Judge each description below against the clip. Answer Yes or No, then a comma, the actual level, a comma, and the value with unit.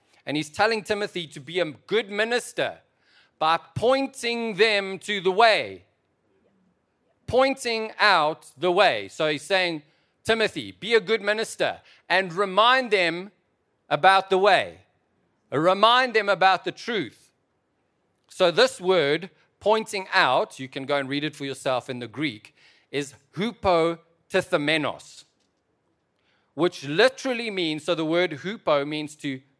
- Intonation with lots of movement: Yes, wide, 5.8 semitones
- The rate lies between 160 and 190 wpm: No, slow, 135 wpm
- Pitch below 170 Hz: No, medium, 180 Hz